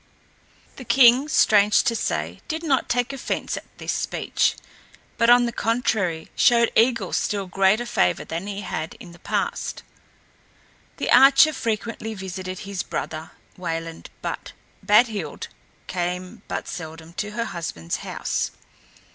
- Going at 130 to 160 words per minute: Yes, slow, 135 wpm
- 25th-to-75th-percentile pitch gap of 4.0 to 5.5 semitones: Yes, average, 5.1 semitones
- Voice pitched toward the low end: No, high, 210 Hz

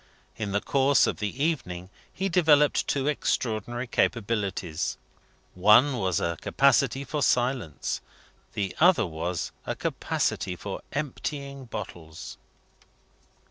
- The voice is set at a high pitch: No, low, 120 Hz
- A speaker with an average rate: No, slow, 110 wpm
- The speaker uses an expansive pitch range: Yes, wide, 6.9 semitones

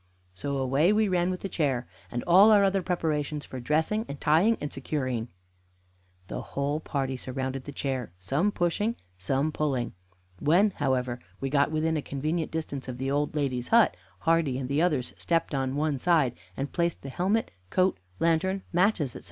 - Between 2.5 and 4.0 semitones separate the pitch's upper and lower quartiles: No, average, 4.6 semitones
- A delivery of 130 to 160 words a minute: No, average, 175 wpm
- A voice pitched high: No, medium, 150 Hz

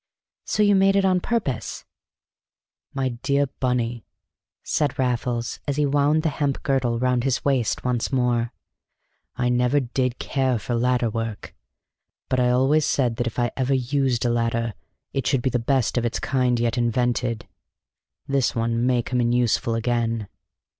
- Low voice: Yes, low, 125 Hz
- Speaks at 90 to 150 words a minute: No, average, 165 wpm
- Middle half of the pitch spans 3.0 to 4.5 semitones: No, narrow, 2.4 semitones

